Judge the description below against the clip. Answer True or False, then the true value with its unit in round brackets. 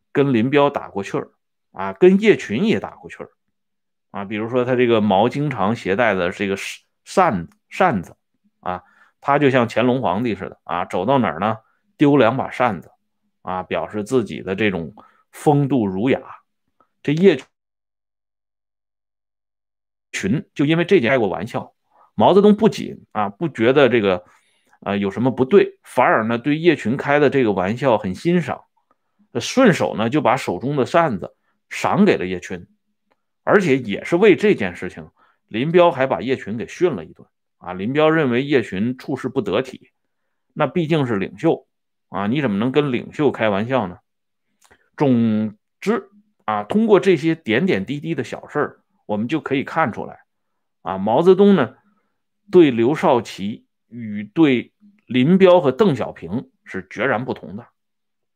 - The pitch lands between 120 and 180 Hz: True (140 Hz)